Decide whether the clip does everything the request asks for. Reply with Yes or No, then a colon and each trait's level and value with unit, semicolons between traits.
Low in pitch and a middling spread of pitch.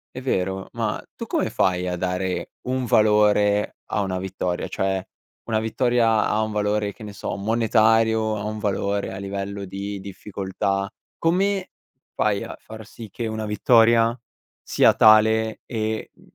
No: low, 105 Hz; narrow, 2.2 semitones